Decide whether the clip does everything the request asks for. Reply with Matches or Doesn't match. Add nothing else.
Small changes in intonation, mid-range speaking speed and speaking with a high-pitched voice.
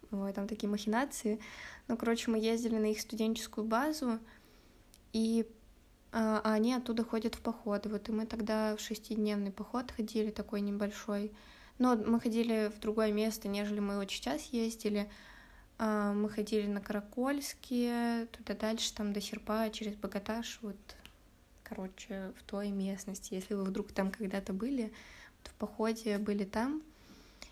Matches